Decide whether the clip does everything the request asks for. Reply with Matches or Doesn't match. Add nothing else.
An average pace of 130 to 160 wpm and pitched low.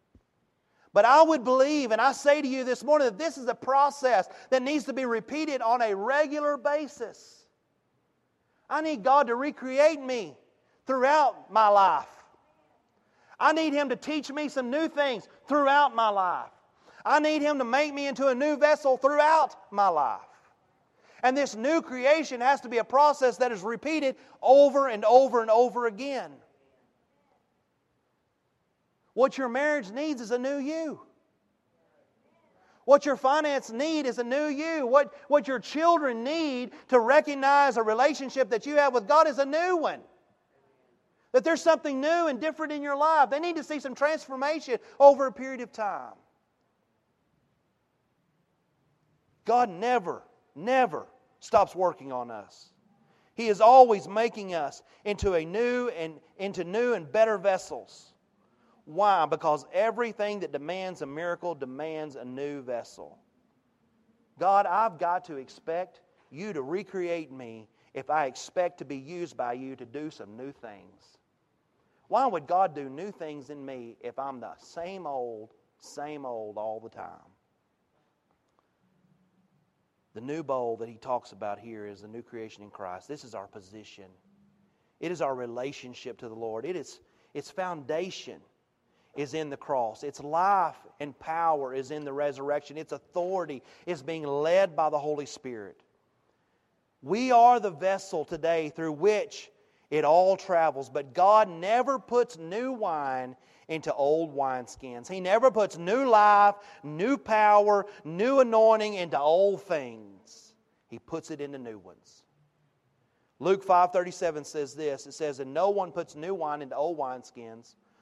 Doesn't match